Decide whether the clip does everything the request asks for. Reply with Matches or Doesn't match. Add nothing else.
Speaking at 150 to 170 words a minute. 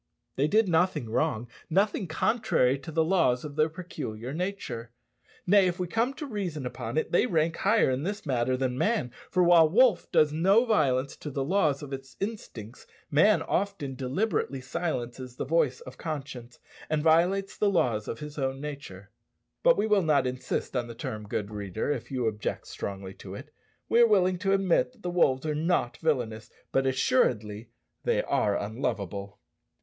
Doesn't match